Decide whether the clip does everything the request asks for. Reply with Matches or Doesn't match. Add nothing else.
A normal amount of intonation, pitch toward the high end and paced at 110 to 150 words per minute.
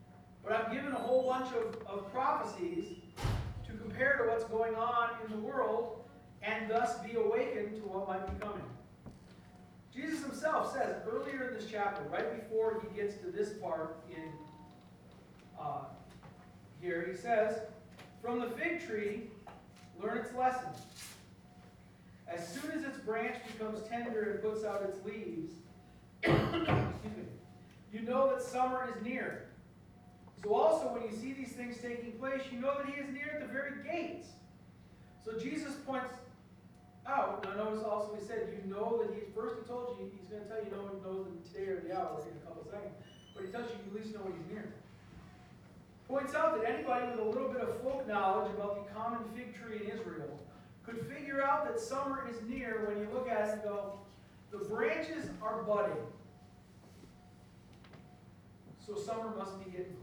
Doesn't match